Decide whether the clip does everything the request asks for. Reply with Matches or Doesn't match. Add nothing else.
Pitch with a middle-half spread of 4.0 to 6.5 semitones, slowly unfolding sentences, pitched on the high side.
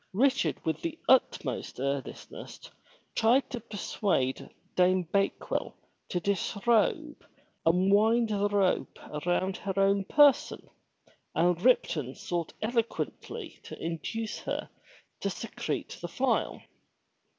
Matches